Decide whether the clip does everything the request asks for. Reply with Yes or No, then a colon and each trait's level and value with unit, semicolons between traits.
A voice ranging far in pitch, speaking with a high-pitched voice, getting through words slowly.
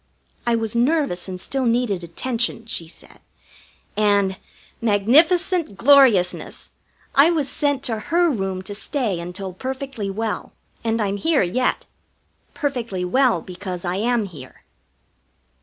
Yes: wide, 5.8 semitones; high, 225 Hz; slow, 125 wpm